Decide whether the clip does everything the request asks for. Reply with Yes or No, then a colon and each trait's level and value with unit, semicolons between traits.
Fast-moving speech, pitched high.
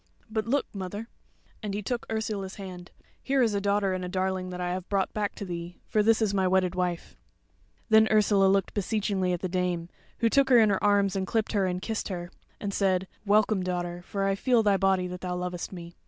Yes: fast, 225 wpm; high, 195 Hz